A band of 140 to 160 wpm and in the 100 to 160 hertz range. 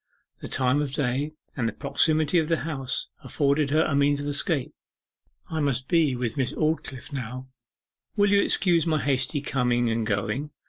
No: average, 175 wpm; medium, 140 Hz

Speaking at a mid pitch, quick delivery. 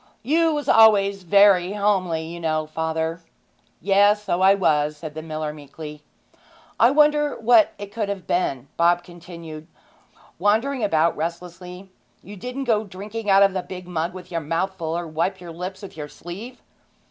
No: medium, 180 Hz; average, 170 wpm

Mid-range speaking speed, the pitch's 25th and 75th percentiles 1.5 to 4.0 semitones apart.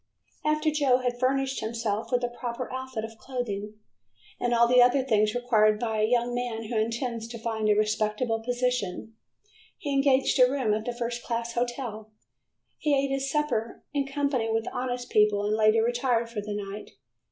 Yes: average, 180 wpm; narrow, 2.6 semitones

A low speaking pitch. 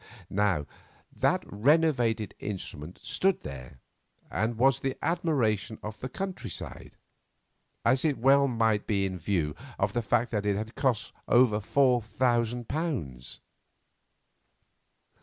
Yes: low, 115 Hz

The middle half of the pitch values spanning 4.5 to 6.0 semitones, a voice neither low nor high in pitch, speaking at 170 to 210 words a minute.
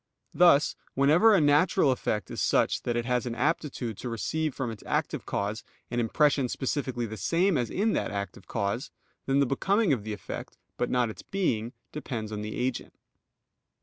No: average, 5.0 semitones; low, 125 Hz; average, 180 wpm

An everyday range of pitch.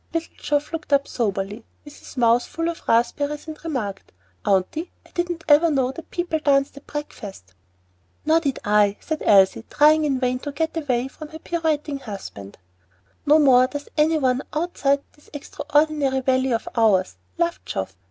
Yes: average, 4.4 semitones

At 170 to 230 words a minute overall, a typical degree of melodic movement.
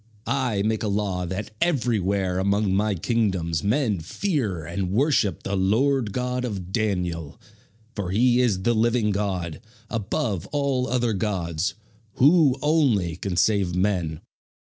No: slow, 135 wpm; average, 4.8 semitones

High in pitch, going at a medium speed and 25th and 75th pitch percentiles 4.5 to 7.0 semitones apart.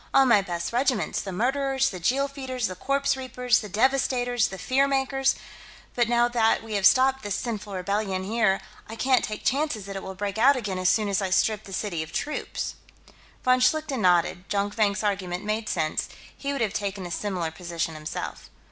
Yes: high, 215 Hz; average, 195 wpm; average, 5.1 semitones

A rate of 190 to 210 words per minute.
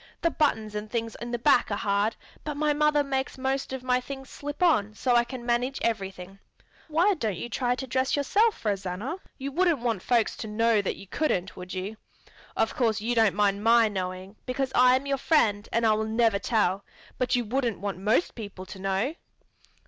Yes: fast, 205 wpm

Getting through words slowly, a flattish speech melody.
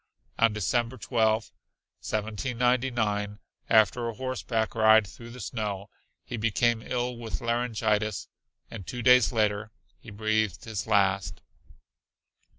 Yes: slow, 115 wpm; narrow, 2.1 semitones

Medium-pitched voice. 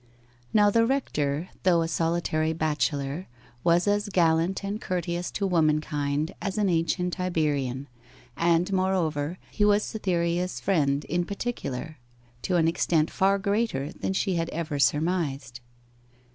Yes: medium, 170 Hz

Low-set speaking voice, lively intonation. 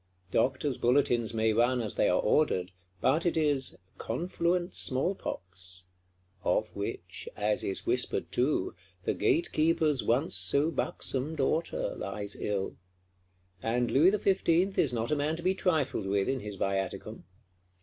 Yes: low, 130 Hz; wide, 8.1 semitones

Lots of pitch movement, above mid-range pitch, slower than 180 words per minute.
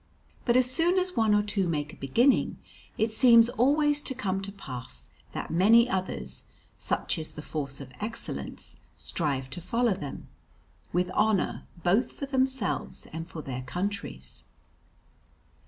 Yes: wide, 8.1 semitones; high, 200 Hz; average, 150 wpm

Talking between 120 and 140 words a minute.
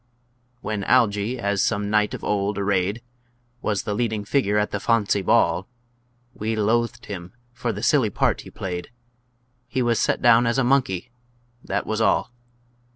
No: average, 160 wpm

